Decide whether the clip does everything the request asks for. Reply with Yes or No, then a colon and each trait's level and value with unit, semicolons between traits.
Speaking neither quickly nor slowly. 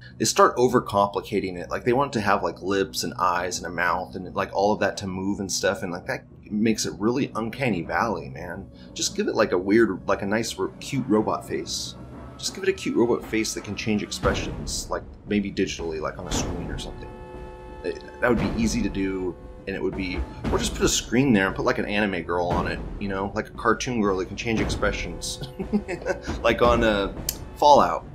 No: fast, 230 wpm